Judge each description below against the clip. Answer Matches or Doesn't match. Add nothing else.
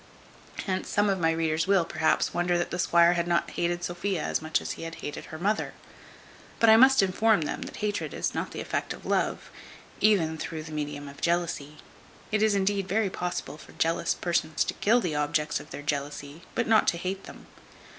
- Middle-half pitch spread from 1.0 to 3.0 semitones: Doesn't match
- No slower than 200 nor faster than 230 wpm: Matches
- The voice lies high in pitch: Doesn't match